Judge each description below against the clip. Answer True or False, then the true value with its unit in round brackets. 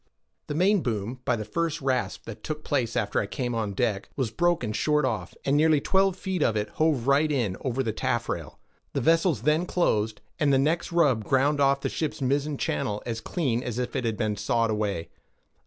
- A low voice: True (130 Hz)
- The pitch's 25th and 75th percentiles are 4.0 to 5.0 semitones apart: False (5.4 semitones)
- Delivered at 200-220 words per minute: True (205 wpm)